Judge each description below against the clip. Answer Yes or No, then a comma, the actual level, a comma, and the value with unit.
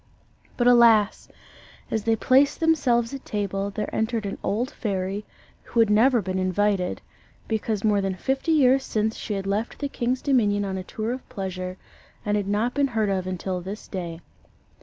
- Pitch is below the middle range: No, high, 210 Hz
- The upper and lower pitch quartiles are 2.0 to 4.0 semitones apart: Yes, average, 3.6 semitones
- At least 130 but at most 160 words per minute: No, average, 180 wpm